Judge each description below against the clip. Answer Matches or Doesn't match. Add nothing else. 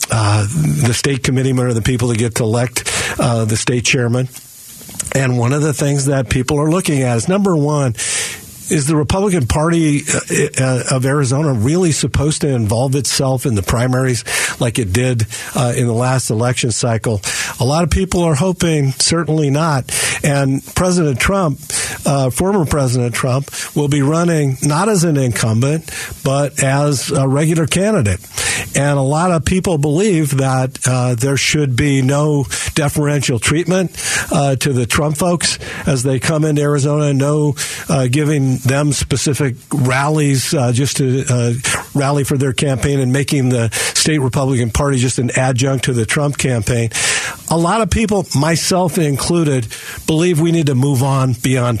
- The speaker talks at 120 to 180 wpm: Matches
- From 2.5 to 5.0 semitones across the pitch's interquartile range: Matches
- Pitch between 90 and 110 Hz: Doesn't match